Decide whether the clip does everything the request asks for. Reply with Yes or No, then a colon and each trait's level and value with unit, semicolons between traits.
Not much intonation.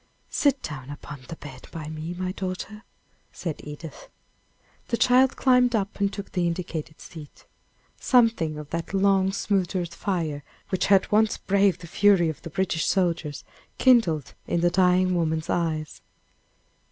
No: average, 3.9 semitones